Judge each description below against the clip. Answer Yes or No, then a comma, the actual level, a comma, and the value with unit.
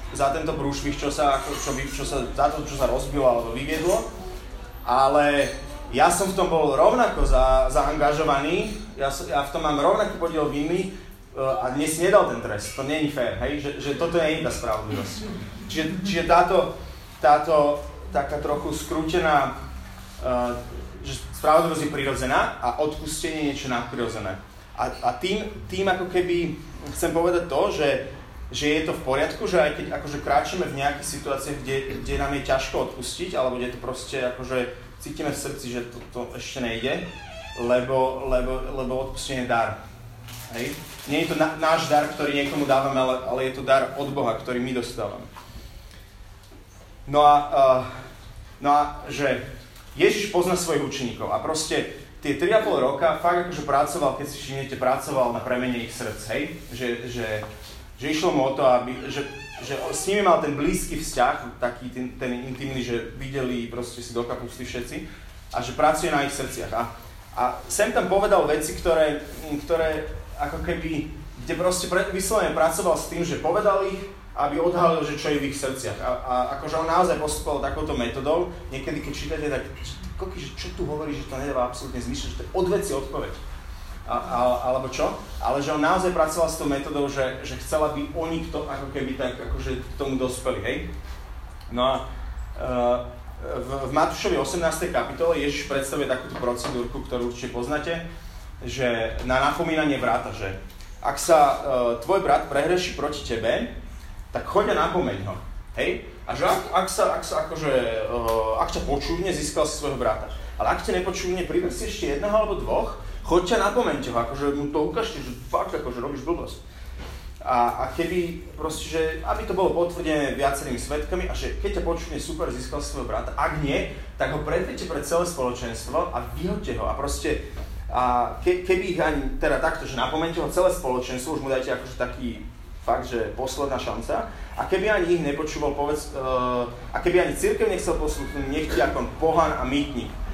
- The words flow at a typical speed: No, fast, 175 wpm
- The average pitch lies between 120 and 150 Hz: Yes, medium, 140 Hz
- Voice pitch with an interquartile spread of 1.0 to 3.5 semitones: No, average, 4.3 semitones